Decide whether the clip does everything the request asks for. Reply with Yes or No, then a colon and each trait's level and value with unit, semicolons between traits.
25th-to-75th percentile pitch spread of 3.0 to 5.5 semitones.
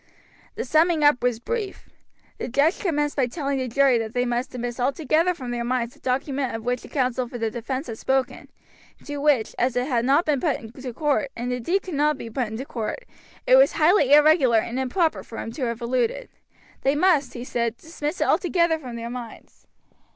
Yes: average, 3.8 semitones